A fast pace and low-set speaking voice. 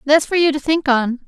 No: fast, 280 wpm; very high, 290 Hz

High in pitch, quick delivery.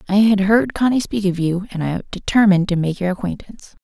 Yes: high, 195 Hz; fast, 220 wpm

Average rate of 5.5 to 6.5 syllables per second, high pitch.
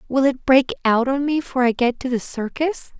No: 4.9 syllables/s; very high, 260 Hz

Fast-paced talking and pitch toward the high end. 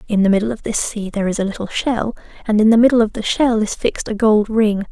Yes: fast, 280 wpm; high, 215 Hz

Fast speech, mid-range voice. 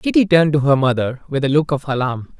Yes: fast, 250 wpm; medium, 145 Hz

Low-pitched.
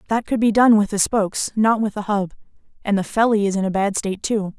No: high, 205 Hz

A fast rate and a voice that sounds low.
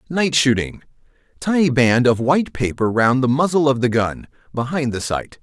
No: average, 175 wpm; low, 130 Hz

